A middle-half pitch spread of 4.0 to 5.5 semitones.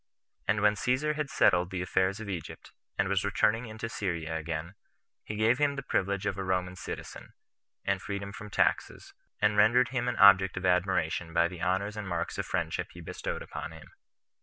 No: average, 3.0 semitones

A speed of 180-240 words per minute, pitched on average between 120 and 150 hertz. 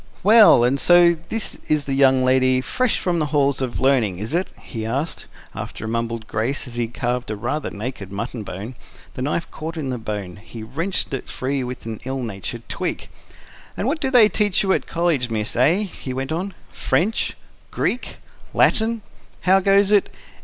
Yes: average, 190 wpm; low, 135 Hz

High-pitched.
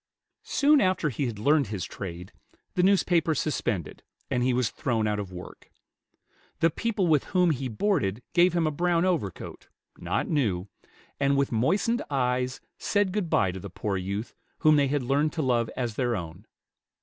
No: low, 135 Hz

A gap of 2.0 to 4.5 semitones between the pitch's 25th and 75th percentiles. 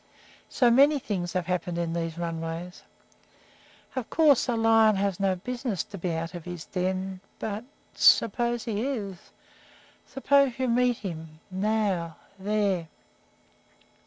No: average, 5.1 semitones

